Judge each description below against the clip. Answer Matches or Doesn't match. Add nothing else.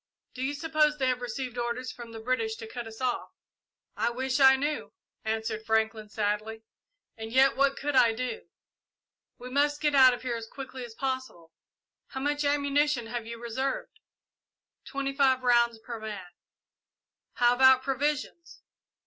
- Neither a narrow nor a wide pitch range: Matches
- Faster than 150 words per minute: Matches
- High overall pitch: Matches